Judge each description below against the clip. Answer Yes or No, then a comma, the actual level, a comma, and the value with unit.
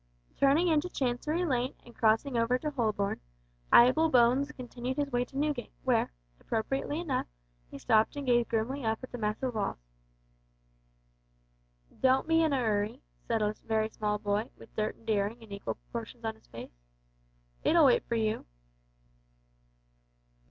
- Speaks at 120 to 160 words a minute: Yes, average, 155 wpm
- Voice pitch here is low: No, high, 240 Hz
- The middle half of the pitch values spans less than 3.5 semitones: No, average, 4.0 semitones